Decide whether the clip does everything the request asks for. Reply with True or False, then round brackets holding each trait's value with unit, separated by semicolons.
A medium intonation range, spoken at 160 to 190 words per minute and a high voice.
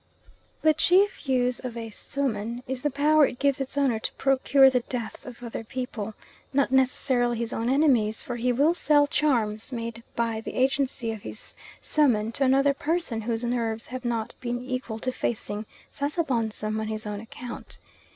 True (3.4 semitones; 175 wpm; 245 Hz)